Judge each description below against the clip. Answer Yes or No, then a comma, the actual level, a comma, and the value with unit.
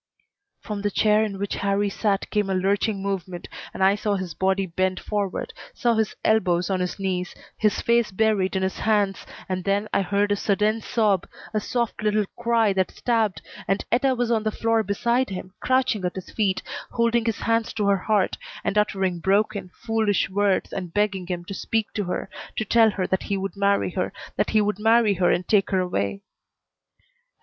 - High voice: Yes, high, 200 Hz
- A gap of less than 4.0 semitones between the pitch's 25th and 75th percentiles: Yes, narrow, 2.5 semitones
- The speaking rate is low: No, average, 195 wpm